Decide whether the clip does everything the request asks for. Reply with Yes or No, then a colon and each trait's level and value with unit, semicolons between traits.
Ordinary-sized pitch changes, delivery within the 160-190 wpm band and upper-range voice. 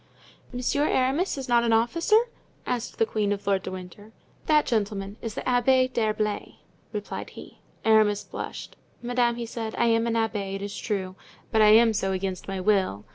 Yes: average, 3.0 semitones; average, 185 wpm; high, 220 Hz